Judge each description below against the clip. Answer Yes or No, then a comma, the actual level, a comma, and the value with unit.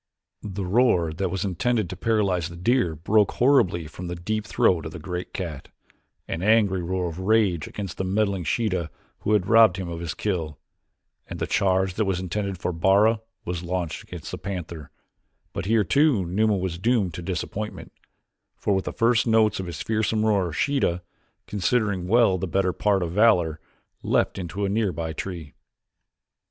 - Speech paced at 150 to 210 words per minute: Yes, average, 180 wpm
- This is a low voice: Yes, very low, 95 Hz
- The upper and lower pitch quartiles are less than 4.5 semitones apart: Yes, average, 3.6 semitones